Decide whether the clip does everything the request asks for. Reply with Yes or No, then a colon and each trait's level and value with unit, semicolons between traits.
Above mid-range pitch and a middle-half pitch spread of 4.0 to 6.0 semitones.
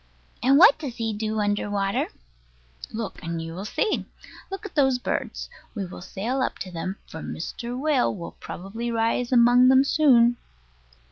Yes: high, 235 Hz; average, 4.7 semitones